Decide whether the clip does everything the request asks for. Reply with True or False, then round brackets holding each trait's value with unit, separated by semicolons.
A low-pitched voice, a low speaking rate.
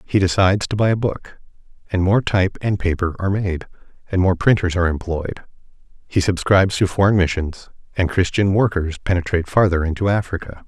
False (90 Hz; 170 wpm)